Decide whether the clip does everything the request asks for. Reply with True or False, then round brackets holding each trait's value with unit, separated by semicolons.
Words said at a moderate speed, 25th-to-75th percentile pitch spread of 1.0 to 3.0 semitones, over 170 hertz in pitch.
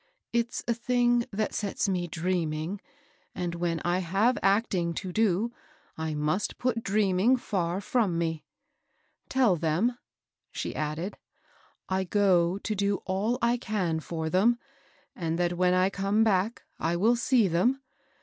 False (150 wpm; 4.6 semitones; 190 Hz)